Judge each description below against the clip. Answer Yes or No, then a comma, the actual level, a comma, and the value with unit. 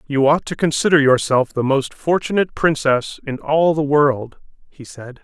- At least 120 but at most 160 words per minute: No, average, 170 wpm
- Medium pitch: Yes, medium, 145 Hz